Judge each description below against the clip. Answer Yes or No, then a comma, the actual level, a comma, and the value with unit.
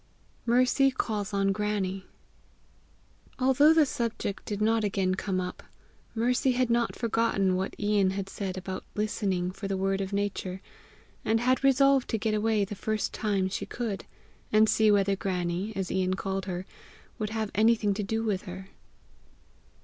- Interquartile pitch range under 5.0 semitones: Yes, average, 2.8 semitones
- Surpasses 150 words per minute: Yes, average, 165 wpm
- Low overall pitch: No, high, 205 Hz